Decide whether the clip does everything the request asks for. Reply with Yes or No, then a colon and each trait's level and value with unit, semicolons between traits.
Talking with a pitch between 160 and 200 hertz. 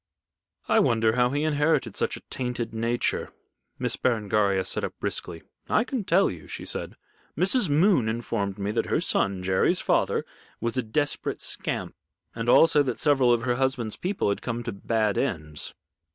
No: low, 120 Hz